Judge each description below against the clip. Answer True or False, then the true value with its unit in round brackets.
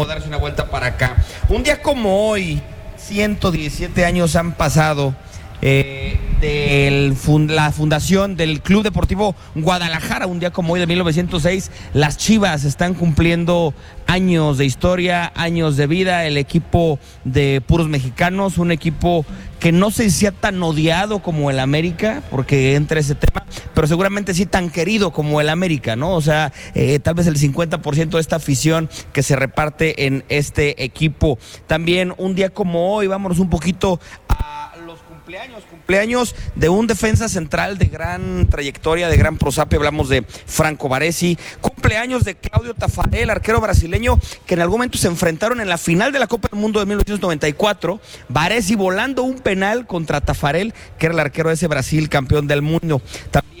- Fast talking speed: False (165 wpm)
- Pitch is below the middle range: False (165 Hz)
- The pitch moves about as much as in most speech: True (4.0 semitones)